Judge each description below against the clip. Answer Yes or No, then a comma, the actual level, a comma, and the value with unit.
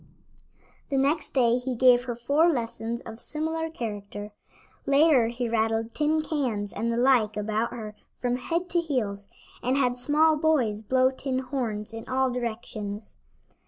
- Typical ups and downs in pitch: Yes, average, 3.8 semitones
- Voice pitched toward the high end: Yes, high, 245 Hz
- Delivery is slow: No, average, 155 wpm